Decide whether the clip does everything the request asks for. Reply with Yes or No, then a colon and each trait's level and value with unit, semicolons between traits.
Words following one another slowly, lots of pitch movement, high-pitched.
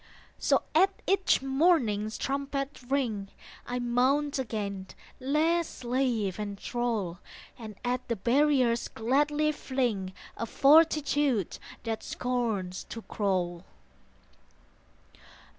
No: slow, 95 wpm; average, 4.8 semitones; high, 245 Hz